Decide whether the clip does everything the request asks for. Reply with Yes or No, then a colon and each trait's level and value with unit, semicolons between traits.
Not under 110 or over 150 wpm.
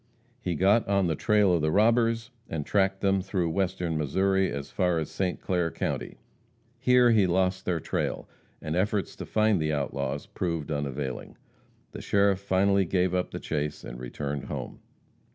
No: average, 170 wpm